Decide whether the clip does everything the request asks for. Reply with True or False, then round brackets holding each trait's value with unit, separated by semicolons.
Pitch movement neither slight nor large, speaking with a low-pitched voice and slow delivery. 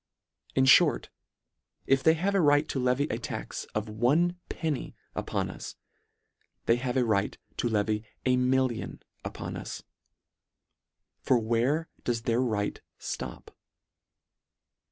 True (3.9 semitones; 125 Hz; 130 wpm)